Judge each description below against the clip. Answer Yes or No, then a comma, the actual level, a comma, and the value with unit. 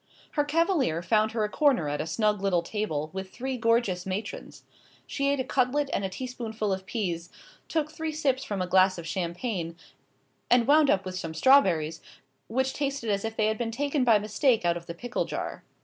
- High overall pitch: Yes, high, 215 Hz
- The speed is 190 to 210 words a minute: Yes, average, 200 wpm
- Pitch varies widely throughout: Yes, wide, 6.1 semitones